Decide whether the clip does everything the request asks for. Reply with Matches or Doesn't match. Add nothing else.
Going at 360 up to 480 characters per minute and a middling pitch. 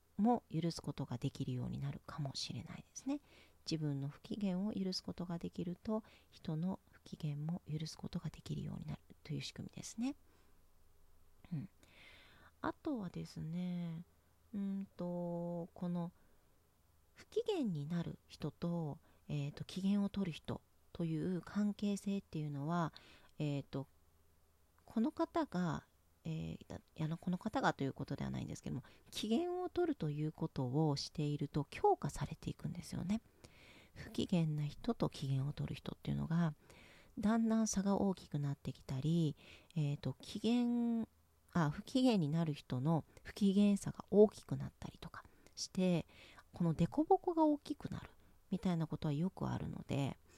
Doesn't match